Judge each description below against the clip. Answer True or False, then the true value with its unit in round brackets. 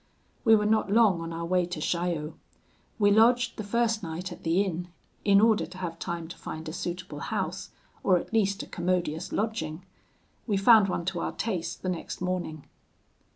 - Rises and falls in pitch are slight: False (3.7 semitones)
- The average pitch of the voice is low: False (185 Hz)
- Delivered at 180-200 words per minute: True (190 wpm)